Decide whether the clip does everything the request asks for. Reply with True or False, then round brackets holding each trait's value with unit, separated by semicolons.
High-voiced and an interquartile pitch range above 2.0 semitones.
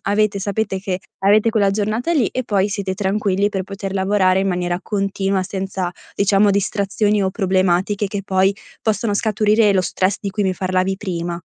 False (195 Hz; 1.6 semitones)